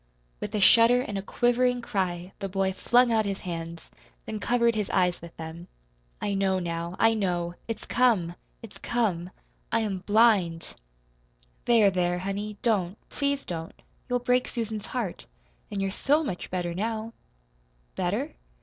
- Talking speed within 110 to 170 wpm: Yes, average, 155 wpm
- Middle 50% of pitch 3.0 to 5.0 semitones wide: Yes, average, 4.4 semitones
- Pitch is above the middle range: Yes, high, 200 Hz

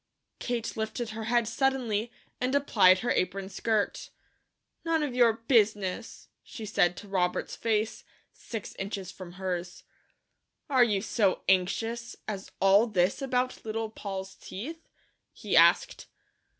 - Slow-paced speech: Yes, slow, 130 wpm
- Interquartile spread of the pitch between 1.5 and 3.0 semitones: No, average, 3.7 semitones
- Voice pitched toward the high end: Yes, high, 220 Hz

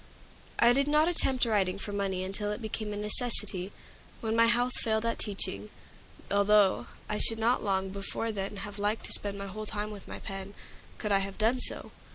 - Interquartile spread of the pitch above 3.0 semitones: No, narrow, 2.4 semitones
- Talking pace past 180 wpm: Yes, average, 195 wpm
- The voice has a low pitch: No, high, 210 Hz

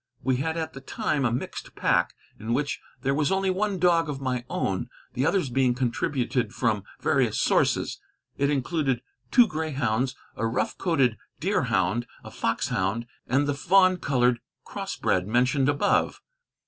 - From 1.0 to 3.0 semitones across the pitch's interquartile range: No, average, 4.4 semitones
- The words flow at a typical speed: Yes, average, 150 wpm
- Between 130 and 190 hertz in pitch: Yes, low, 135 Hz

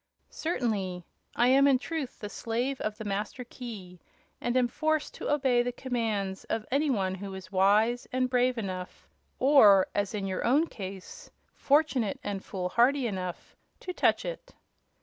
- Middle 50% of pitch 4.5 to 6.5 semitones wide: Yes, average, 4.9 semitones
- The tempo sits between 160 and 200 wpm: Yes, average, 165 wpm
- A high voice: Yes, high, 230 Hz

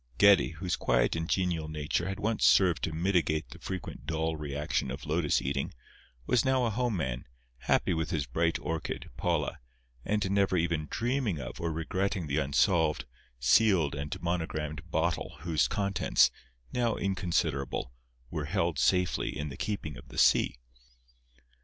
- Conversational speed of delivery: Yes, average, 155 wpm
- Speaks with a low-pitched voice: Yes, very low, 85 Hz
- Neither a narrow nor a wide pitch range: Yes, average, 4.2 semitones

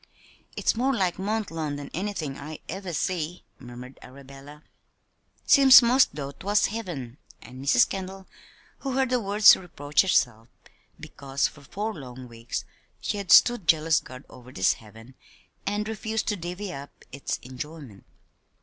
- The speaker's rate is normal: Yes, average, 150 wpm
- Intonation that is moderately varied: No, wide, 7.2 semitones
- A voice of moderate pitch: Yes, medium, 160 Hz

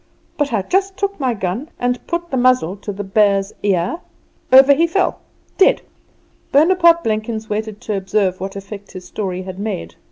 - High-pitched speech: Yes, high, 215 Hz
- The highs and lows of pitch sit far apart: Yes, wide, 6.6 semitones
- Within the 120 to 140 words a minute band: No, average, 170 wpm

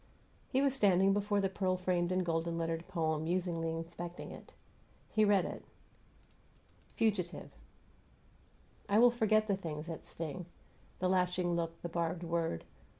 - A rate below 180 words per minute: Yes, average, 145 wpm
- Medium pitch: Yes, medium, 180 Hz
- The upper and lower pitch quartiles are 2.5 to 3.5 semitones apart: Yes, average, 2.8 semitones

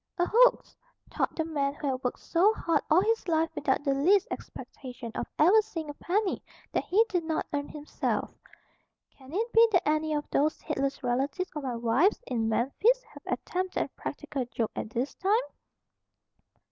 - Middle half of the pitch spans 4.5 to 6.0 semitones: Yes, wide, 5.6 semitones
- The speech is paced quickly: No, average, 180 wpm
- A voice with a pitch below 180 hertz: No, very high, 310 Hz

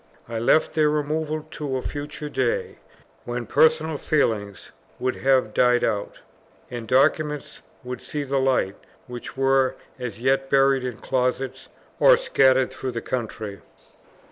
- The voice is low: Yes, low, 130 Hz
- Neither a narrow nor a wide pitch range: Yes, average, 3.1 semitones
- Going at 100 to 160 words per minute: Yes, average, 140 wpm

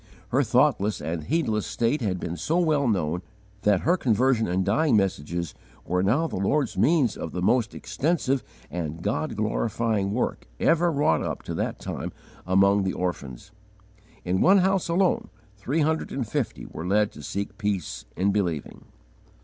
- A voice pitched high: No, low, 105 Hz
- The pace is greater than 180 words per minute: No, average, 165 wpm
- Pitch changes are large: Yes, wide, 7.6 semitones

